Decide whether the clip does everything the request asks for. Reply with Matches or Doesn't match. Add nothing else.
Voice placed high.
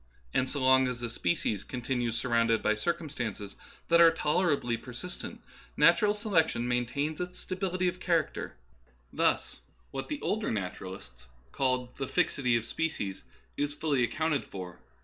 Doesn't match